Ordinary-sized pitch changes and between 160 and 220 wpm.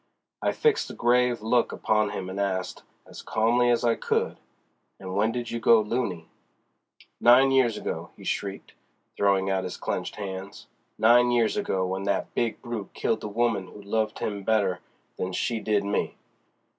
Yes: average, 3.4 semitones; average, 170 wpm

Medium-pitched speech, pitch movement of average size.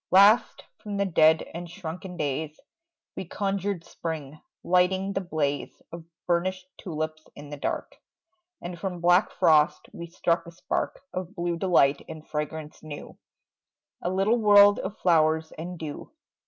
Yes: medium, 170 Hz; average, 3.1 semitones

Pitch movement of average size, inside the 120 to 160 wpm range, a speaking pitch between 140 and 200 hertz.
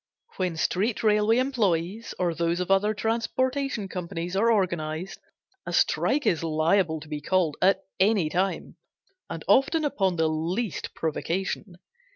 Yes: average, 4.8 semitones; average, 140 wpm; high, 190 Hz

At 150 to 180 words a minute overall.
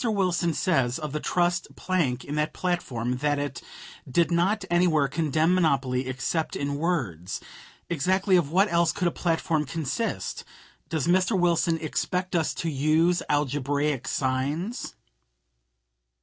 No: slow, 135 wpm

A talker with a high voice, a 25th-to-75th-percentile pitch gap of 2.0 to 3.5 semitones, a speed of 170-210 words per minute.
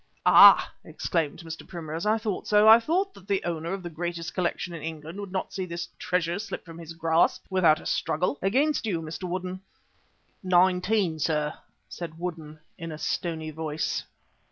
No: medium, 175 Hz; average, 2.7 semitones; average, 175 wpm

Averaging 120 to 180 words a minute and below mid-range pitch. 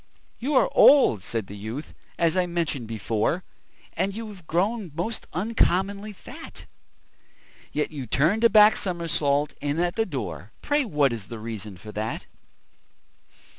No: average, 150 wpm; medium, 165 Hz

